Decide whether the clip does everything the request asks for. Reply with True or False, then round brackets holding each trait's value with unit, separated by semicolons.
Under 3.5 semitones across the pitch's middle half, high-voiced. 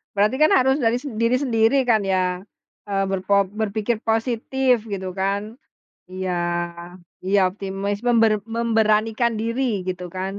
True (3.0 semitones; 220 Hz)